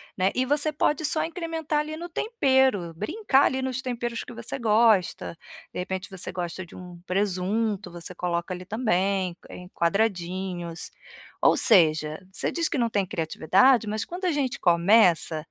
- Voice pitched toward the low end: No, high, 205 Hz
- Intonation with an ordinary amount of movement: No, wide, 6.8 semitones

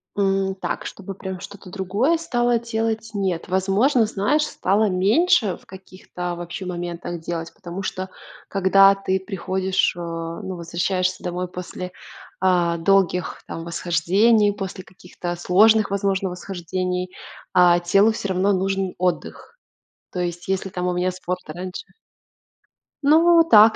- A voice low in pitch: No, high, 190 Hz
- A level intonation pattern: Yes, narrow, 2.1 semitones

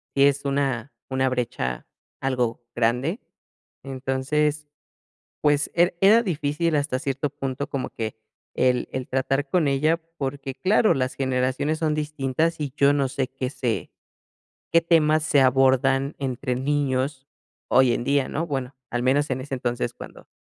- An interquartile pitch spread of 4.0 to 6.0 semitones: No, narrow, 2.4 semitones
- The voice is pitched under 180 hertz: Yes, low, 135 Hz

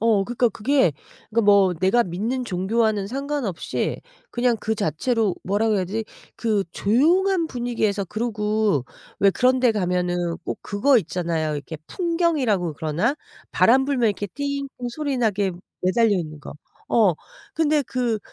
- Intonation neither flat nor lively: Yes, average, 4.9 semitones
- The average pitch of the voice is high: Yes, high, 220 Hz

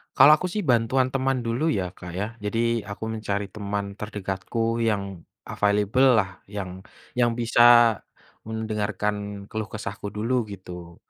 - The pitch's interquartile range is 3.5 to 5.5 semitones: No, average, 2.7 semitones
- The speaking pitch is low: Yes, low, 105 Hz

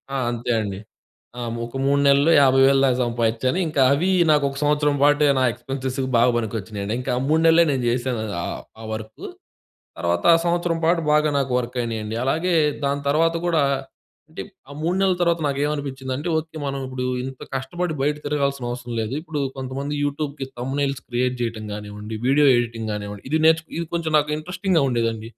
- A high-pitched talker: No, low, 135 Hz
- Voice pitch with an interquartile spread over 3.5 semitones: Yes, average, 4.0 semitones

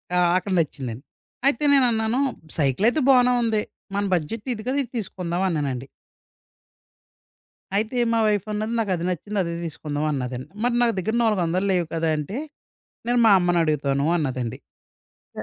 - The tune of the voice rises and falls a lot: Yes, wide, 6.7 semitones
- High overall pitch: No, medium, 180 Hz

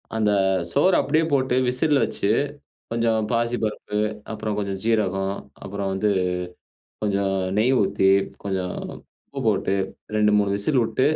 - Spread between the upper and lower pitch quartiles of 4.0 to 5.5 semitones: No, average, 3.4 semitones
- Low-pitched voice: Yes, low, 105 Hz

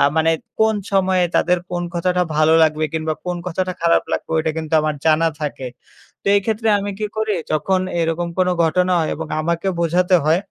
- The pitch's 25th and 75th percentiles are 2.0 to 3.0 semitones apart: Yes, narrow, 2.5 semitones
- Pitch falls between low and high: Yes, medium, 170 Hz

